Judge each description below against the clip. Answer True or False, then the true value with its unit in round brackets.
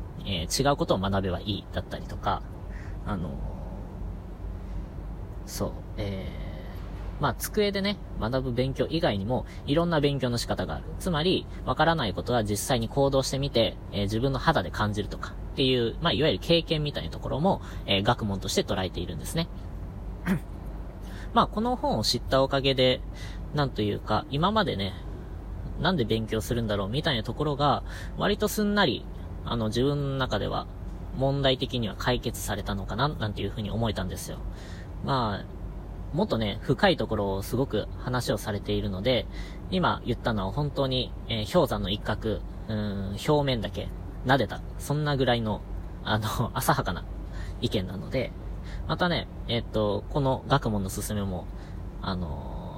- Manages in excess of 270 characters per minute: True (325 characters per minute)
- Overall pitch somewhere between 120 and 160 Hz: False (105 Hz)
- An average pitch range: False (5.7 semitones)